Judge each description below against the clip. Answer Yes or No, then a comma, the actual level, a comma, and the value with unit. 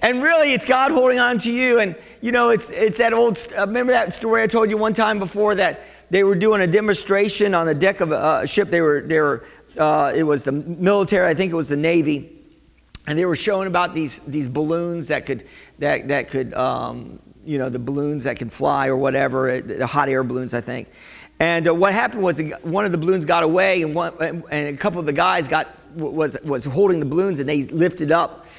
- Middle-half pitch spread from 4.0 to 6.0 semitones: Yes, wide, 5.6 semitones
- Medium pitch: Yes, medium, 170 Hz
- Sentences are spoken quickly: Yes, fast, 235 wpm